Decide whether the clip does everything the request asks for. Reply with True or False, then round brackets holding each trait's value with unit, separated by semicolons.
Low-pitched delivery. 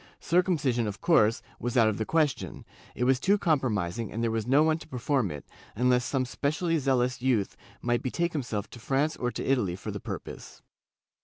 True (125 Hz)